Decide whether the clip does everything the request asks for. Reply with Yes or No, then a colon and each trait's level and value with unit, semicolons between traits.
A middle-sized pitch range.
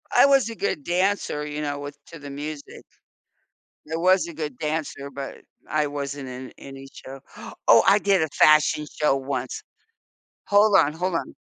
Yes: average, 3.8 semitones